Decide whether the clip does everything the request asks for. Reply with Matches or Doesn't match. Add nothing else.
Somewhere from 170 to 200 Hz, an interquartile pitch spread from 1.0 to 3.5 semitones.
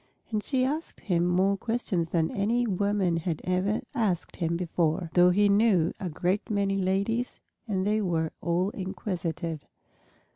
Matches